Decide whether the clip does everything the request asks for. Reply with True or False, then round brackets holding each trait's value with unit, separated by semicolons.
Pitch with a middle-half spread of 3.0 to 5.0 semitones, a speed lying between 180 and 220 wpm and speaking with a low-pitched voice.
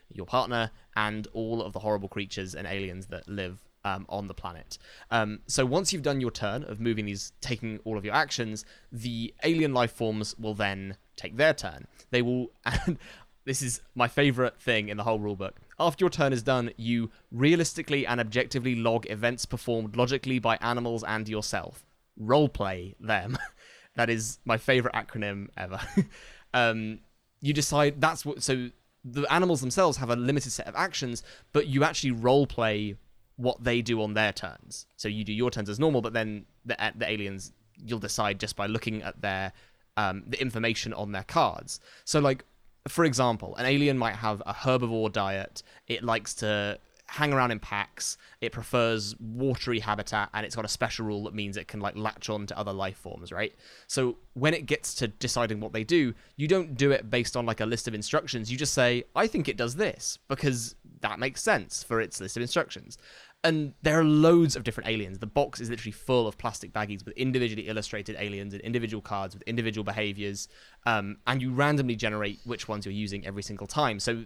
True (3.3 semitones; 200 wpm; 115 Hz)